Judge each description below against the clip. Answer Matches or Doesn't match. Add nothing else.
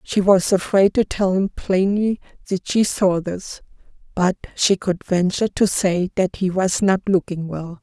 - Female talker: Matches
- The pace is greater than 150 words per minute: Matches